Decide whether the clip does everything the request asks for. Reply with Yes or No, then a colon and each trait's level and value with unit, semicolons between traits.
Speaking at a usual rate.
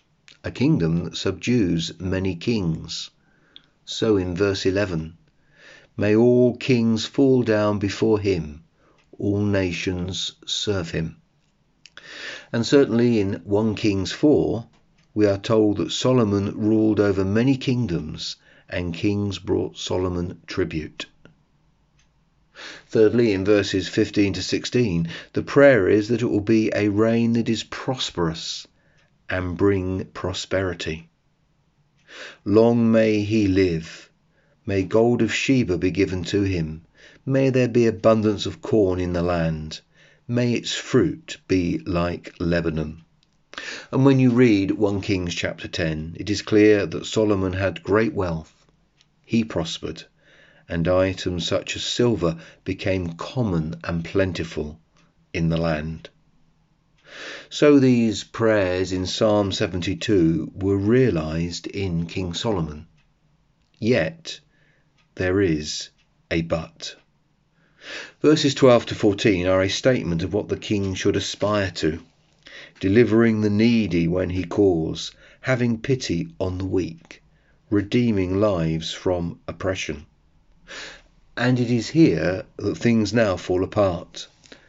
No: slow, 125 wpm